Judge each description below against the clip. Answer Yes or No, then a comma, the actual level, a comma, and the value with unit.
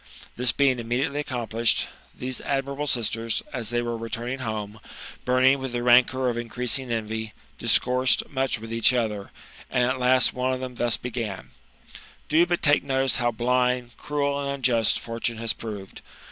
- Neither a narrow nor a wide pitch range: No, narrow, 2.2 semitones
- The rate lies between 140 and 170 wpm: Yes, average, 165 wpm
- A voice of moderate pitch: No, low, 125 Hz